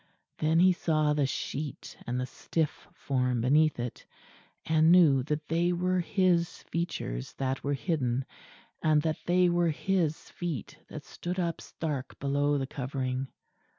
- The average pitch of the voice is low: No, medium, 155 Hz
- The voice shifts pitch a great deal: No, average, 4.2 semitones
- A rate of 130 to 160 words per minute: Yes, average, 150 wpm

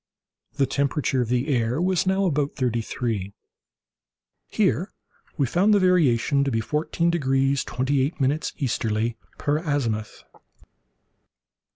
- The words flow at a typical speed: No, slow, 115 wpm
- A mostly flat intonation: No, average, 4.3 semitones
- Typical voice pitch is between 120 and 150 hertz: Yes, medium, 140 Hz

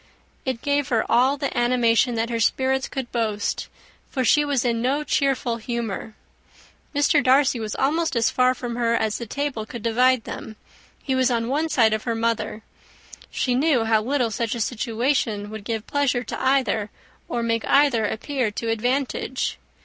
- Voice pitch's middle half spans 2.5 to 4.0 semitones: Yes, average, 2.8 semitones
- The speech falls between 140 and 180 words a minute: Yes, average, 175 wpm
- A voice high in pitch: Yes, high, 245 Hz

